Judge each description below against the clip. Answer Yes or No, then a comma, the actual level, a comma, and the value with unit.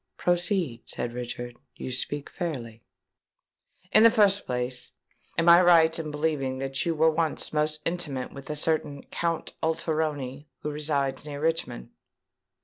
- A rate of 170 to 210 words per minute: No, average, 140 wpm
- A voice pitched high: No, medium, 150 Hz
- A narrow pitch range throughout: No, average, 3.6 semitones